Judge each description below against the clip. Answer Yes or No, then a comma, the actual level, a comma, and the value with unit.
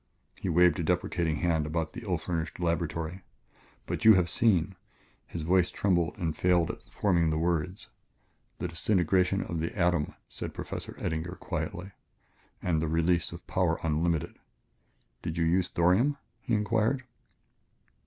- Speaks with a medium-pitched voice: No, very low, 85 Hz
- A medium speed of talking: Yes, average, 160 wpm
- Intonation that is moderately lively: No, narrow, 2.1 semitones